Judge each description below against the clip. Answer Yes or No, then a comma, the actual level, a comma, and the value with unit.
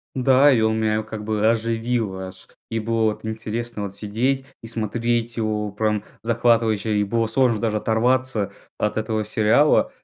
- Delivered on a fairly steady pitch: Yes, narrow, 1.6 semitones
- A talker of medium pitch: No, low, 110 Hz